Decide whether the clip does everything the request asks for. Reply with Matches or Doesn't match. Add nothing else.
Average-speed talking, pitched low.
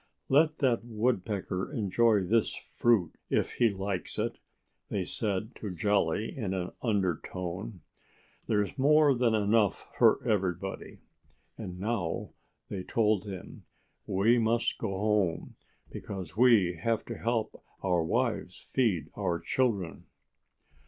Doesn't match